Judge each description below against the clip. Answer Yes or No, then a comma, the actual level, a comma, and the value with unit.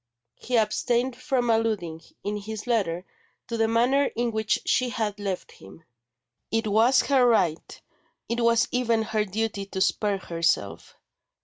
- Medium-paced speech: Yes, average, 145 wpm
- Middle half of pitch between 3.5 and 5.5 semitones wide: No, average, 3.0 semitones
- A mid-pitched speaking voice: No, high, 220 Hz